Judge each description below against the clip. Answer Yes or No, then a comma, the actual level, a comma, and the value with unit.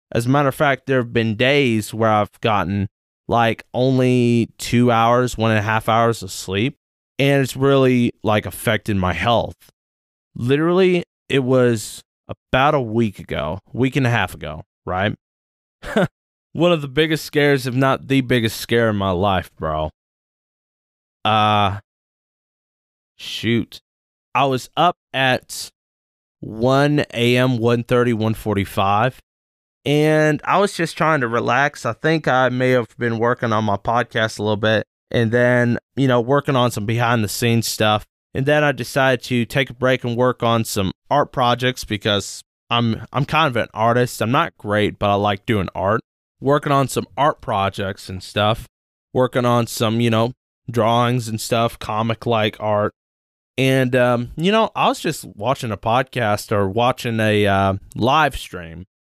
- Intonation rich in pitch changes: No, average, 3.8 semitones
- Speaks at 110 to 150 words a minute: No, average, 160 wpm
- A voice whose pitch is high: No, low, 115 Hz